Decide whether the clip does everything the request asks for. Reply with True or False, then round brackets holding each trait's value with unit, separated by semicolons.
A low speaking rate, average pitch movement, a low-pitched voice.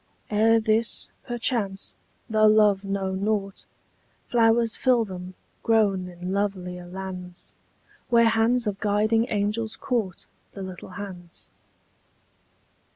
False (105 wpm; 3.0 semitones; 205 Hz)